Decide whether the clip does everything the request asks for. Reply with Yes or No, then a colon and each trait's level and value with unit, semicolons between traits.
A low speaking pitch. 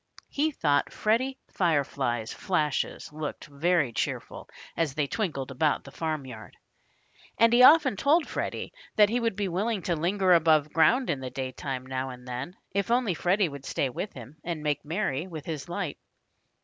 No: medium, 160 Hz